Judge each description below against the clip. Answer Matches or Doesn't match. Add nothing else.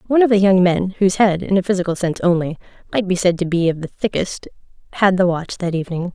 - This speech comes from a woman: Matches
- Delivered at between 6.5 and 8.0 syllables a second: Matches